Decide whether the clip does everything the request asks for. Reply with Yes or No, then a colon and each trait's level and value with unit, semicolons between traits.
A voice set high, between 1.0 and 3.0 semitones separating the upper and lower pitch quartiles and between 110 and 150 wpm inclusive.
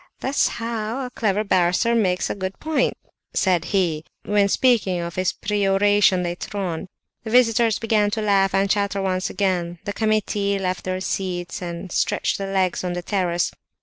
No: high, 195 Hz; narrow, 2.6 semitones; average, 170 wpm